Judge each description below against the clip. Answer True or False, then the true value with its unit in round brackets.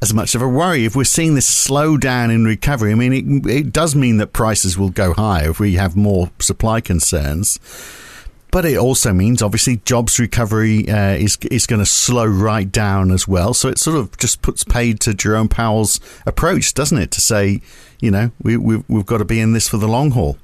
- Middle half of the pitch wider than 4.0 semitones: False (3.3 semitones)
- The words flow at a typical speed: False (225 wpm)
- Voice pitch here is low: True (110 Hz)